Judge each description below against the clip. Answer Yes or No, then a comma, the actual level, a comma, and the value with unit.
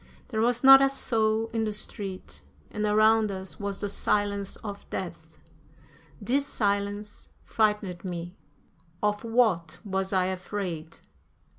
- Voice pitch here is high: Yes, high, 205 Hz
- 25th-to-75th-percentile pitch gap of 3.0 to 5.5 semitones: No, narrow, 2.6 semitones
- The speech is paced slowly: Yes, slow, 130 wpm